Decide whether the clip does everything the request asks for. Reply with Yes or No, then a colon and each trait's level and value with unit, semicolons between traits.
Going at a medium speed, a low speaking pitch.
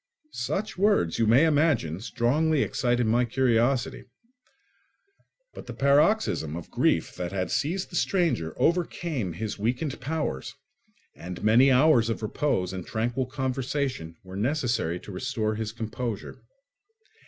No: slow, 130 wpm; low, 120 Hz